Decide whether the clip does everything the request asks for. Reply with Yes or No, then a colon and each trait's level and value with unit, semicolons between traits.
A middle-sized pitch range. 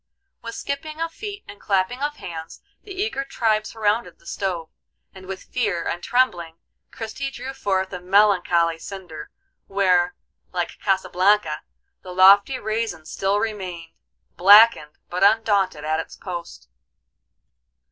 Yes: average, 4.5 semitones